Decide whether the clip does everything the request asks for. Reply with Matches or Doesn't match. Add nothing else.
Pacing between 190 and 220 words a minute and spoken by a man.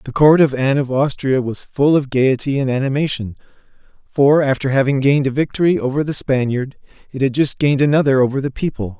Matches